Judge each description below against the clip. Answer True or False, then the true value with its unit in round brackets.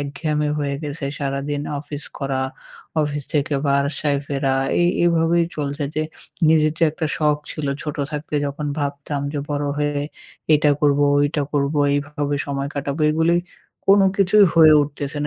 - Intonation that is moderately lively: False (1.4 semitones)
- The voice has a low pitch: False (145 Hz)